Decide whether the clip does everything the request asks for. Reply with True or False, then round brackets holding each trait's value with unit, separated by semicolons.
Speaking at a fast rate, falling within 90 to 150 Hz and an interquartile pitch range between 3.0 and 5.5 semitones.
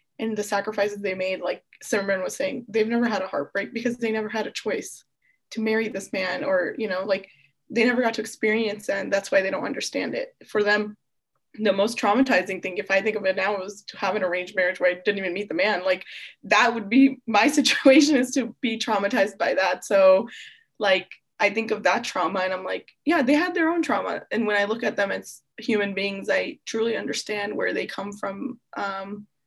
False (225 wpm; 210 Hz; 3.6 semitones)